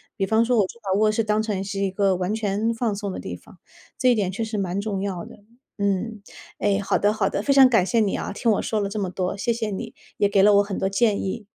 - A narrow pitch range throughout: Yes, narrow, 2.2 semitones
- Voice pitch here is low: No, high, 205 Hz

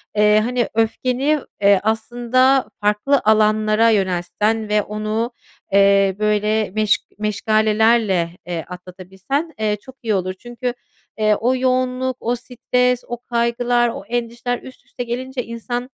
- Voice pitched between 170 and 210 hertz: No, high, 225 Hz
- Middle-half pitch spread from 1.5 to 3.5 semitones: Yes, average, 2.7 semitones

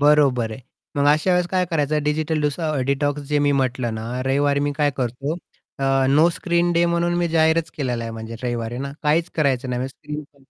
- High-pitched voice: No, medium, 145 Hz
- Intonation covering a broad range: No, average, 3.4 semitones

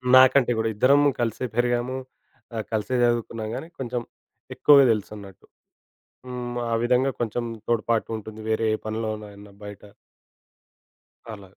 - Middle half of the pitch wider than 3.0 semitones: No, narrow, 2.5 semitones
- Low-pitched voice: Yes, low, 115 Hz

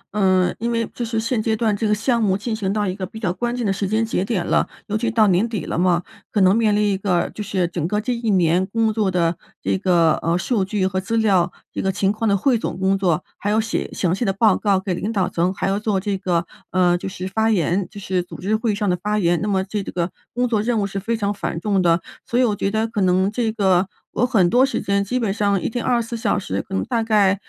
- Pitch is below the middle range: No, high, 200 Hz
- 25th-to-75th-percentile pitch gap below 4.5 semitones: Yes, average, 2.9 semitones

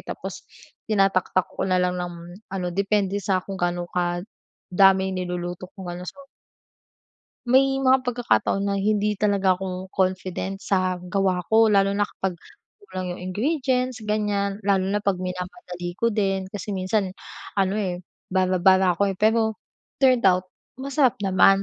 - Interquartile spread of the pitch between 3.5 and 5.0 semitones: No, narrow, 2.4 semitones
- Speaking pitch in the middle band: No, high, 195 Hz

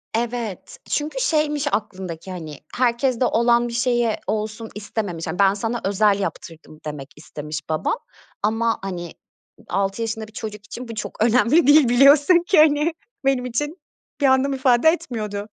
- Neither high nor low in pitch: No, high, 230 Hz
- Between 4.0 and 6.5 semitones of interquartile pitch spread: Yes, average, 4.8 semitones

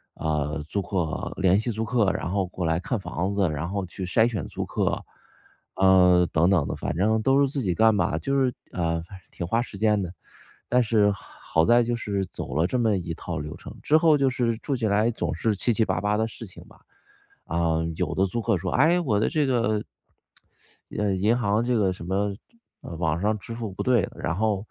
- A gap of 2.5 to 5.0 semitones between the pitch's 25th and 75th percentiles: Yes, average, 4.4 semitones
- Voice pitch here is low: Yes, low, 100 Hz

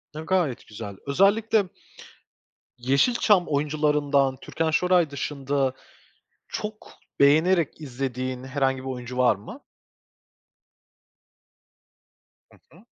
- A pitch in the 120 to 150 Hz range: Yes, medium, 140 Hz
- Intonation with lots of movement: No, average, 4.6 semitones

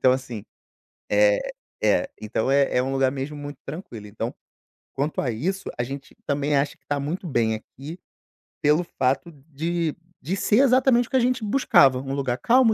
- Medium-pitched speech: Yes, medium, 145 Hz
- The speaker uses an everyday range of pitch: No, wide, 6.6 semitones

